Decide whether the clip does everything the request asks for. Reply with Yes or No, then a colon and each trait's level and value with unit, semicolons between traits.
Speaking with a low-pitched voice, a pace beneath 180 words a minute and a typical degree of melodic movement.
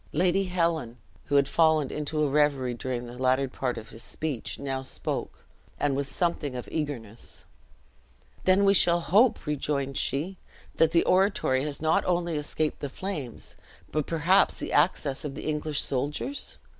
No: medium, 150 Hz; average, 160 wpm; average, 4.0 semitones